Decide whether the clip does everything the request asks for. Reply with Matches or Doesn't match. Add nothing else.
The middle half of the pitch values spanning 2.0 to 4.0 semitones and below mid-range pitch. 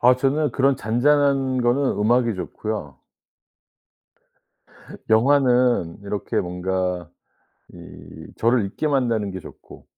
Doesn't match